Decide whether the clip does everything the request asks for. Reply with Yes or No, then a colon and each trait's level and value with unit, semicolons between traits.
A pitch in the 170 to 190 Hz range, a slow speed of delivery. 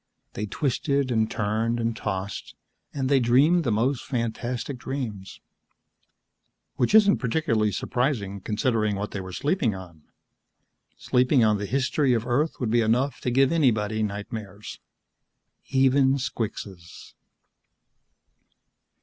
No: low, 120 Hz; slow, 120 wpm